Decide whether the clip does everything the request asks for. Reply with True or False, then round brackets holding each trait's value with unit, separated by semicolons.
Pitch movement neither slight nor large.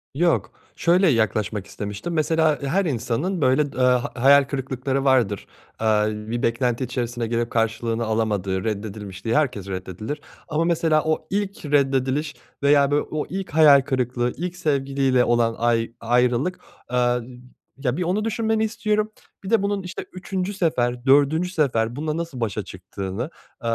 False (5.7 semitones)